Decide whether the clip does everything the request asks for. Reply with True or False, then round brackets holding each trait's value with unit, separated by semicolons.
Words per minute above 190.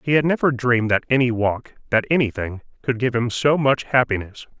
False (170 wpm)